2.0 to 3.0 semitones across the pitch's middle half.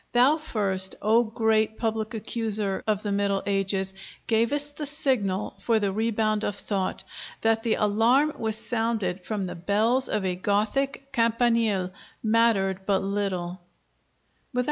Yes: average, 2.7 semitones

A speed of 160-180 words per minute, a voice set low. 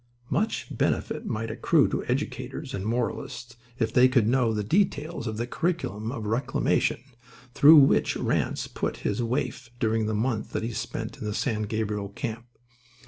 Yes: average, 165 wpm; low, 115 Hz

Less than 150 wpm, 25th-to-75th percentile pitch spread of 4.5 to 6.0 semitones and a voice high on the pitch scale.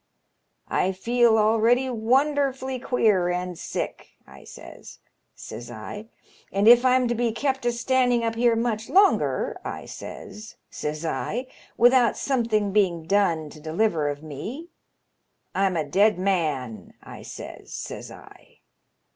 Yes: average, 140 wpm; wide, 5.6 semitones; high, 220 Hz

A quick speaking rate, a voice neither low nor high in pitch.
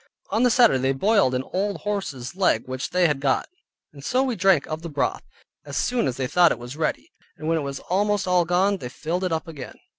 Yes: fast, 240 wpm; medium, 165 Hz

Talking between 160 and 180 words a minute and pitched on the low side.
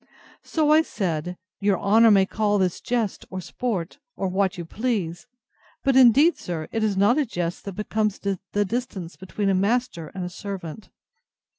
No: average, 170 wpm; high, 200 Hz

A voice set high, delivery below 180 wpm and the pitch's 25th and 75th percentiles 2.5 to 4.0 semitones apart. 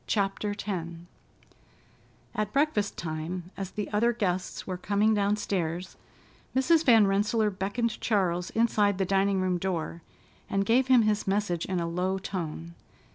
Yes: high, 195 Hz; average, 140 wpm; average, 2.8 semitones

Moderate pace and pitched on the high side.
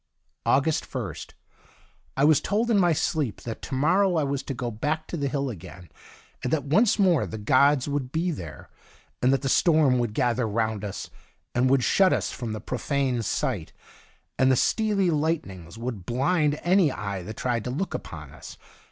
No: average, 190 wpm; low, 135 Hz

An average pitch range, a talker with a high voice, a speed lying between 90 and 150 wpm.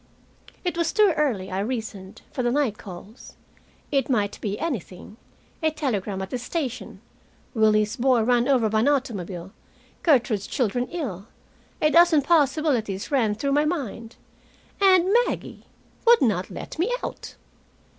No: wide, 6.2 semitones; high, 245 Hz; average, 145 wpm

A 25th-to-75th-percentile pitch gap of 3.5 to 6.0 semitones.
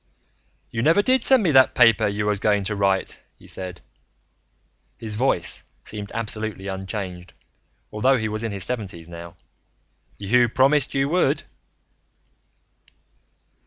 Yes: average, 4.4 semitones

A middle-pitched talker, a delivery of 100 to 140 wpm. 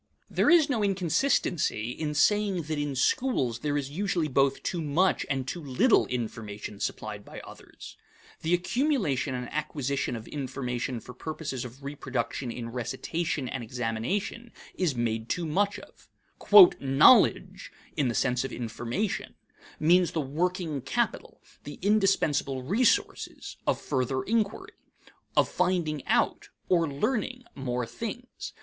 Yes: medium, 145 Hz; slow, 135 wpm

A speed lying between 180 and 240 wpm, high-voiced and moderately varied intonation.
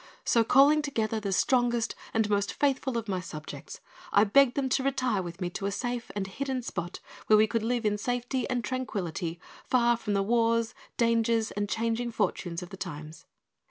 Yes: average, 190 wpm; high, 225 Hz; average, 3.7 semitones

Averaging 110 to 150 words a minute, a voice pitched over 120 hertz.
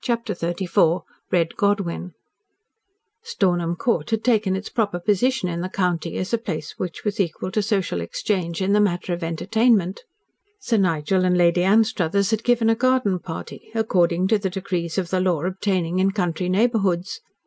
No: average, 170 wpm; medium, 185 Hz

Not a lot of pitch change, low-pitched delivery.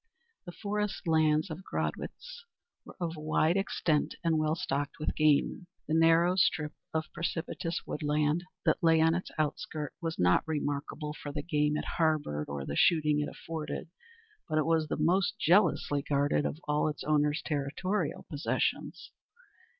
No: narrow, 2.0 semitones; medium, 155 Hz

